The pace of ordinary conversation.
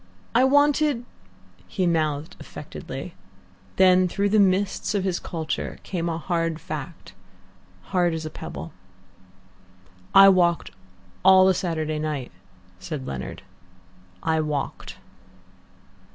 No: slow, 115 wpm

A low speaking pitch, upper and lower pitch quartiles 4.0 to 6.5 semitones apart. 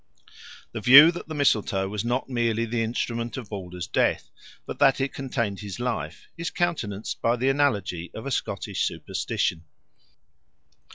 Yes: low, 115 Hz; average, 4.8 semitones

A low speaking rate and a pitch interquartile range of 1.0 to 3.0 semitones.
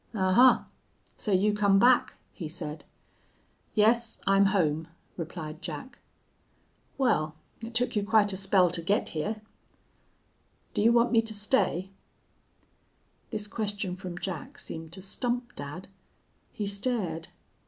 No: slow, 130 wpm; average, 4.2 semitones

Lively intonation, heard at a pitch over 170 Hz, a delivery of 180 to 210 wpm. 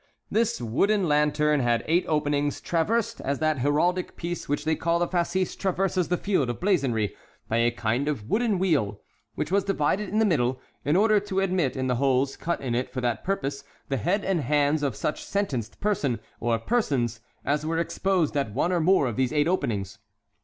No: wide, 6.1 semitones; medium, 150 Hz; average, 195 wpm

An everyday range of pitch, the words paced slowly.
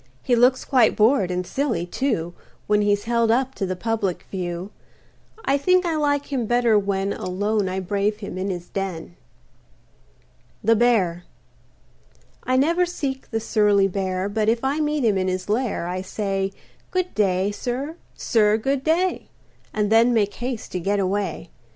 No: average, 4.9 semitones; average, 165 wpm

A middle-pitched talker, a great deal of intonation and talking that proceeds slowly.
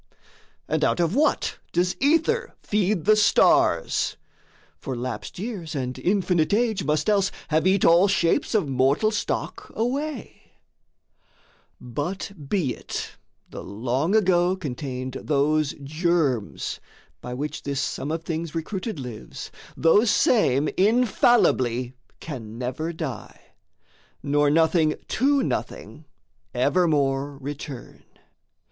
Yes: medium, 165 Hz; wide, 6.5 semitones; slow, 115 wpm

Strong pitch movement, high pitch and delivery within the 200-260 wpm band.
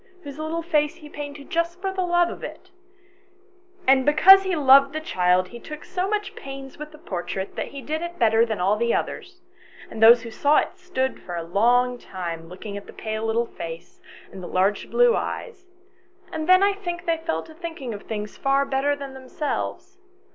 Yes: wide, 7.2 semitones; very high, 275 Hz; fast, 205 wpm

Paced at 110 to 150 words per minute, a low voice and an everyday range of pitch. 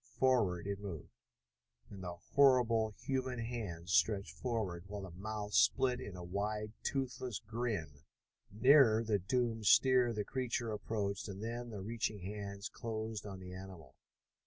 Yes: average, 145 wpm; low, 105 Hz; average, 3.4 semitones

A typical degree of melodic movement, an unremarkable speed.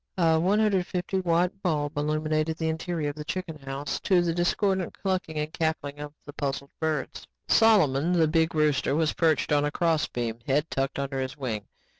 Yes: average, 3.1 semitones; average, 185 wpm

